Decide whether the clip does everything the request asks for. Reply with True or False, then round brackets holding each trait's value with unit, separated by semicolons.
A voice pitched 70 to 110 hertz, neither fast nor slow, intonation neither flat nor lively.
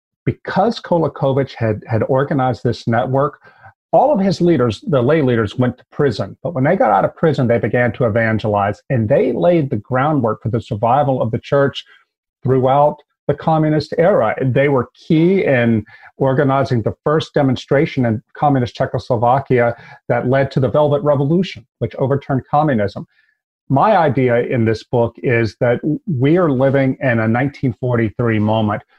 False (130 Hz; 160 wpm; 3.7 semitones)